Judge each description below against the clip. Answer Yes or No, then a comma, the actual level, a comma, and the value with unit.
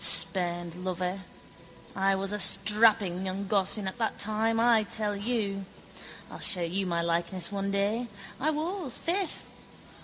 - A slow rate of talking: No, average, 145 wpm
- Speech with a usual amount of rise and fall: Yes, average, 3.3 semitones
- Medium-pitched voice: No, high, 200 Hz